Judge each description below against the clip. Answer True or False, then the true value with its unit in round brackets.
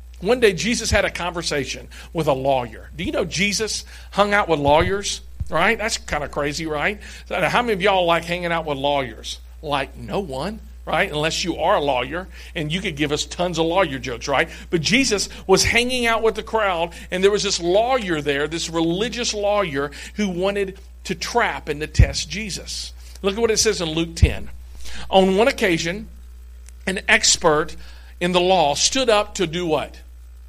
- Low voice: False (170 Hz)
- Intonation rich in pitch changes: True (6.2 semitones)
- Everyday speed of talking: True (190 wpm)